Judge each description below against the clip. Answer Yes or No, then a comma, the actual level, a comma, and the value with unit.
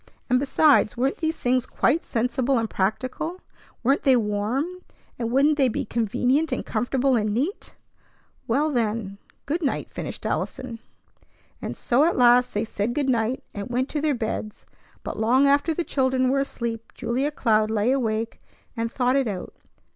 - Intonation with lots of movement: No, average, 3.6 semitones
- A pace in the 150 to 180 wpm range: Yes, average, 165 wpm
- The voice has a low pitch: No, very high, 250 Hz